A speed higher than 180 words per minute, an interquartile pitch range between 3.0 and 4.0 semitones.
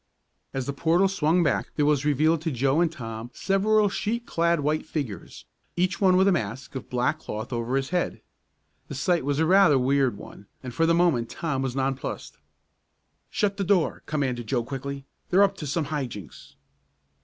No: average, 190 wpm; average, 4.8 semitones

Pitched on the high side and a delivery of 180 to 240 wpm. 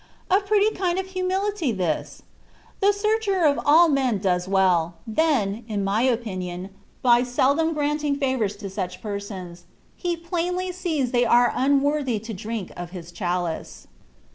No: very high, 250 Hz; average, 165 wpm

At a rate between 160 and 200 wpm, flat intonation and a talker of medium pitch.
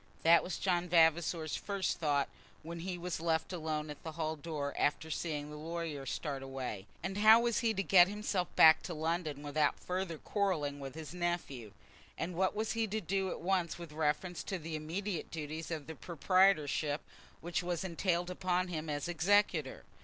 No: average, 180 wpm; average, 3.2 semitones; medium, 165 Hz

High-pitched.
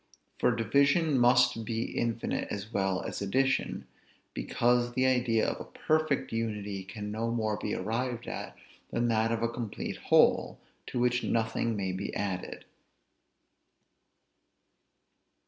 No: low, 115 Hz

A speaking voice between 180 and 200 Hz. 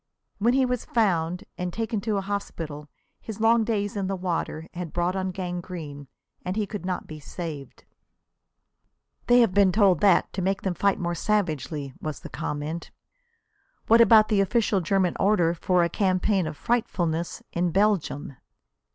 Yes: medium, 185 Hz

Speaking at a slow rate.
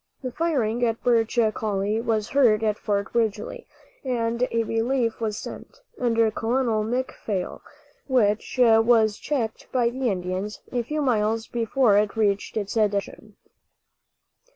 Yes: slow, 130 wpm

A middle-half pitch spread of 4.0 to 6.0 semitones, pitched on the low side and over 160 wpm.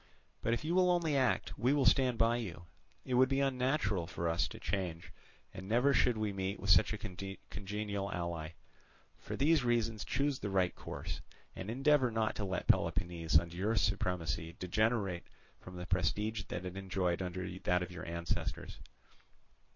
Yes: average, 5.3 semitones; low, 100 Hz; average, 175 wpm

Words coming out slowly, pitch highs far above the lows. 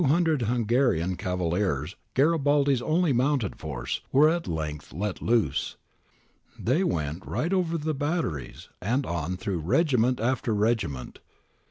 Yes: slow, 130 wpm; wide, 8.7 semitones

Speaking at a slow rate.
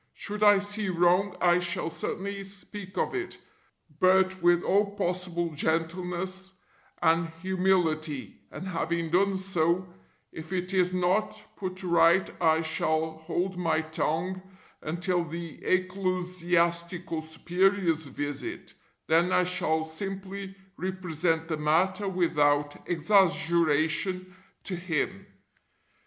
Yes: slow, 110 wpm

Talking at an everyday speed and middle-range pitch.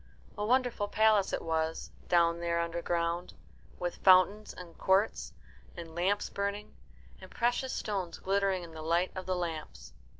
Yes: average, 145 wpm; medium, 180 Hz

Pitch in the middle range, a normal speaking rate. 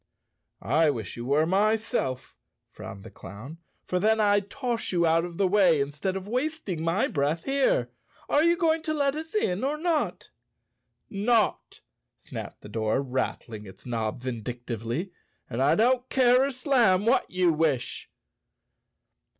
Yes: medium, 180 Hz; average, 155 wpm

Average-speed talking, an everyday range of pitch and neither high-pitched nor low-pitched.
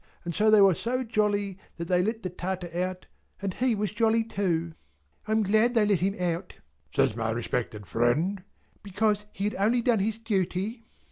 No: average, 190 wpm; average, 3.5 semitones; high, 200 Hz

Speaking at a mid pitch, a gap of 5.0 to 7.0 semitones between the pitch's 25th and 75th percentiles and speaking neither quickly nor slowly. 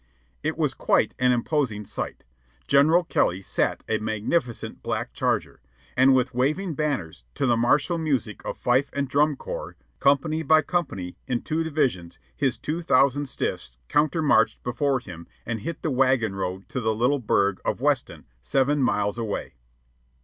No: low, 130 Hz; average, 5.3 semitones; average, 155 wpm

